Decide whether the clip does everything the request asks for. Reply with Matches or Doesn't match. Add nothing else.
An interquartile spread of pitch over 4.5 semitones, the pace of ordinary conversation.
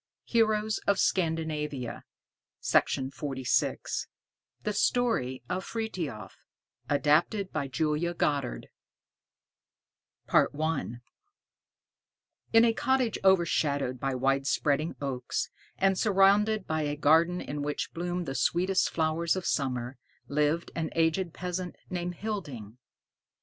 Doesn't match